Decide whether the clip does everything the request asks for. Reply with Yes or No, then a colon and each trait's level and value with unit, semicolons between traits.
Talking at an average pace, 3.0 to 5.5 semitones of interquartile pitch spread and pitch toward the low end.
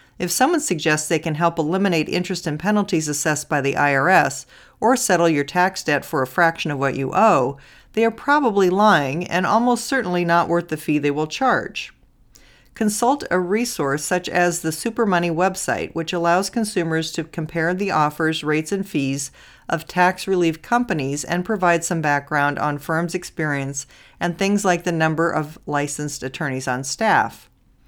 No: average, 170 wpm; average, 3.8 semitones; medium, 170 Hz